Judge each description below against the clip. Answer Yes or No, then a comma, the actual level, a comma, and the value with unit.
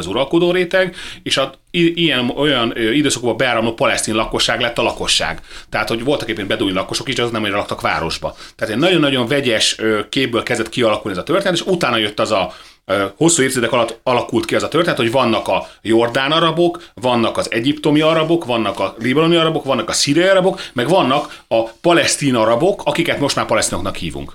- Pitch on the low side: Yes, low, 130 Hz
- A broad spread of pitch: Yes, wide, 6.5 semitones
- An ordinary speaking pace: No, fast, 190 wpm